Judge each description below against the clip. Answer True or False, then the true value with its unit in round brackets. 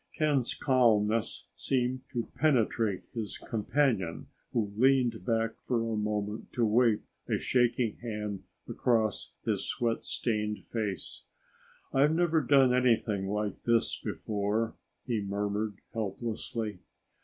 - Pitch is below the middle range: True (115 Hz)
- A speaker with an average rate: False (115 wpm)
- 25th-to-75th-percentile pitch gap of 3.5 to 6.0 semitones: False (2.9 semitones)